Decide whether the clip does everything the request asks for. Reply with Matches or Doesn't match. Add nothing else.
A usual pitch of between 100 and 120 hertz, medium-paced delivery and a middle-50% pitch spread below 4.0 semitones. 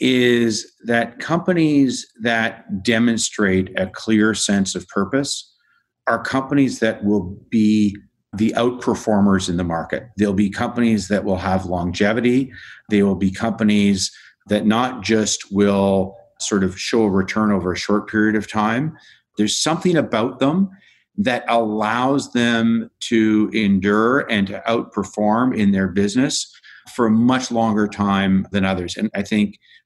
Matches